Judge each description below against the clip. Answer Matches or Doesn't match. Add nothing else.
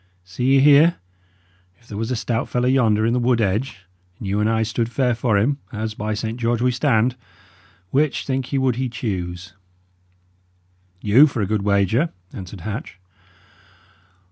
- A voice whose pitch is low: Matches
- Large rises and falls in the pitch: Doesn't match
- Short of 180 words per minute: Matches